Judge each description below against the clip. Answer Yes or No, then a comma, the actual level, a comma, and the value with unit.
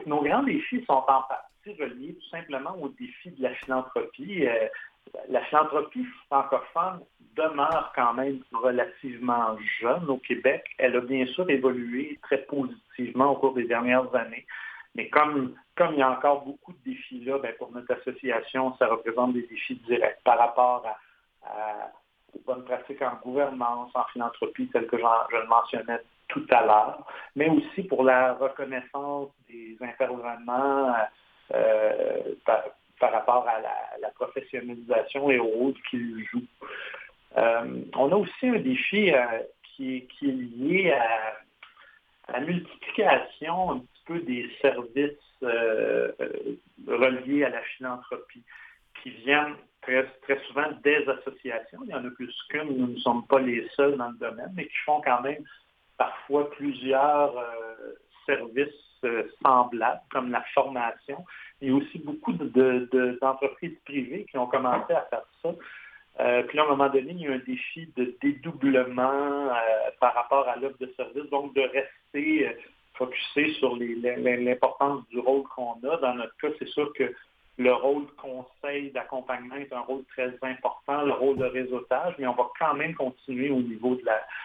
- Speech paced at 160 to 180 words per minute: Yes, average, 170 wpm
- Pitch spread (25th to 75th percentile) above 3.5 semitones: No, average, 2.9 semitones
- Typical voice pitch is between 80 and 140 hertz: Yes, low, 135 Hz